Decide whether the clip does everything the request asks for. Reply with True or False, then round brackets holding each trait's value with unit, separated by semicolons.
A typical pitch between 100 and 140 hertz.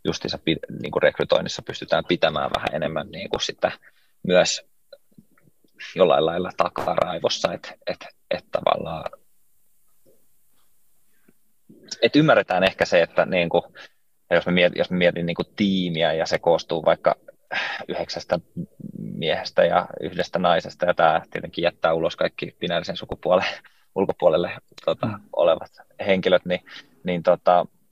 False (90 Hz)